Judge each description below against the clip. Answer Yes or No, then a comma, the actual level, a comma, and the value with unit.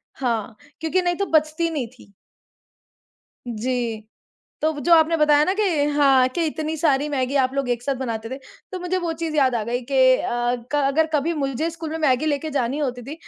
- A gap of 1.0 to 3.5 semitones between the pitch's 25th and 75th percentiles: No, average, 4.0 semitones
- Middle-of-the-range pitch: No, very high, 285 Hz